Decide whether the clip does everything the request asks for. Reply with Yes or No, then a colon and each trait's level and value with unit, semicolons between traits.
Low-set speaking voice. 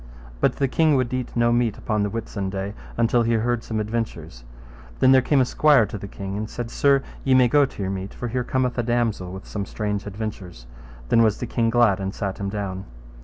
Yes: low, 110 Hz